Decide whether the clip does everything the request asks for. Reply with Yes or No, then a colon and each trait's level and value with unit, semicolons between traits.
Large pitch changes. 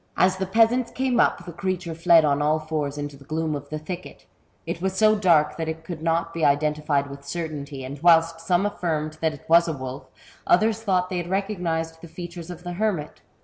No: average, 3.1 semitones